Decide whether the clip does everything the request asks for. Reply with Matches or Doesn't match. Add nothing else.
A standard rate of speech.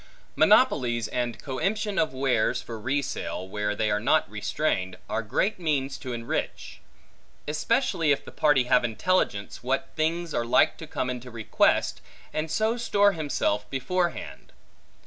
Matches